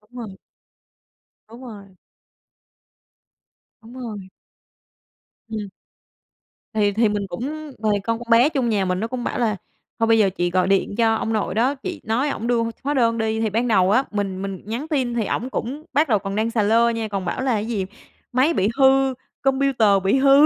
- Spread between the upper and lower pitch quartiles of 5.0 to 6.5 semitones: No, average, 3.8 semitones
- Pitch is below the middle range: No, high, 225 Hz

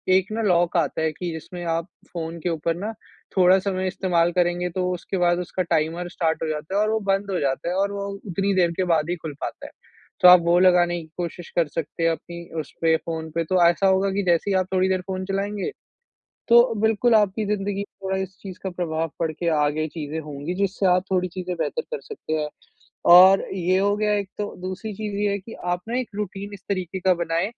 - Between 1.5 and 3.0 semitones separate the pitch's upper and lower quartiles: Yes, average, 2.7 semitones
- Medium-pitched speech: Yes, medium, 180 Hz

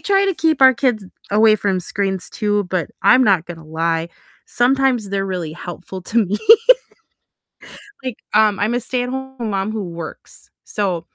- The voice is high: Yes, high, 205 Hz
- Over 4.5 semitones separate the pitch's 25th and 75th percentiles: Yes, average, 5.2 semitones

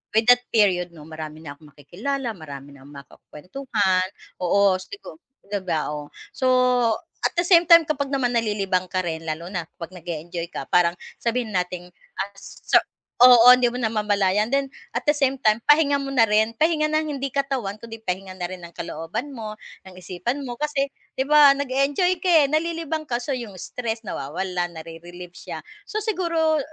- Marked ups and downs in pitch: Yes, wide, 7.6 semitones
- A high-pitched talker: Yes, high, 215 Hz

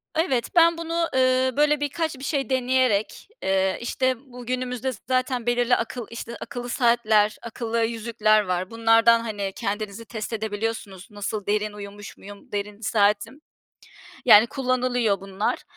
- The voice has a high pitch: Yes, high, 230 Hz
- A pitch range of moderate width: Yes, average, 3.5 semitones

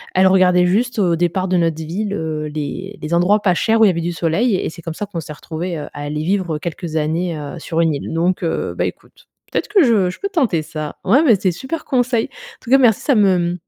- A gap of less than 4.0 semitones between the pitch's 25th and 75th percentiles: No, average, 4.6 semitones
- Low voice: No, medium, 180 Hz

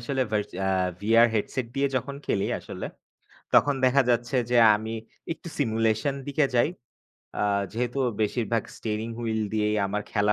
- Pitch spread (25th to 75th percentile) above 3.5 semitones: No, average, 3.2 semitones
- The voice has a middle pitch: No, low, 115 Hz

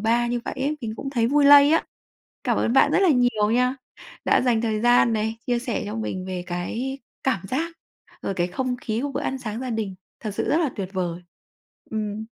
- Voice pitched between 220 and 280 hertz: Yes, high, 235 Hz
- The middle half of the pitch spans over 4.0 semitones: No, average, 3.7 semitones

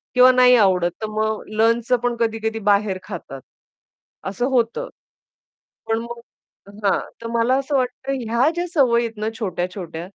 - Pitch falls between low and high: No, high, 225 Hz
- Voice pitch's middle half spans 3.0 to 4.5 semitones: Yes, average, 3.5 semitones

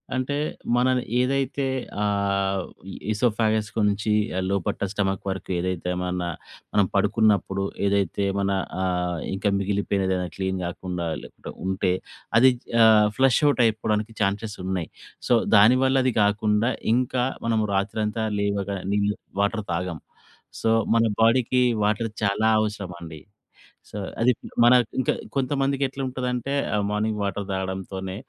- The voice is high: No, low, 105 Hz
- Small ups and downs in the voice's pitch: No, average, 3.1 semitones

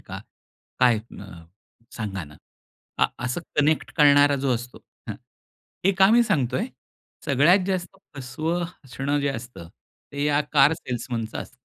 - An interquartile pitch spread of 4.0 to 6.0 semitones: Yes, average, 4.6 semitones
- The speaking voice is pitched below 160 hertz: Yes, medium, 140 Hz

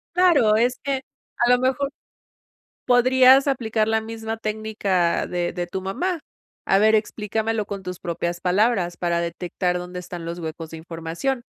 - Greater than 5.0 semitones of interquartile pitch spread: Yes, wide, 5.4 semitones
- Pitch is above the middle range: Yes, high, 210 Hz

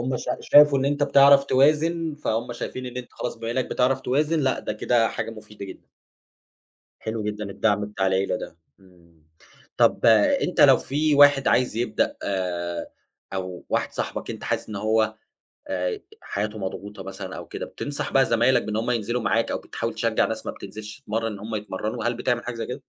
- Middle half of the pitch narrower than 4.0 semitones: No, average, 4.3 semitones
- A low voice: Yes, low, 115 Hz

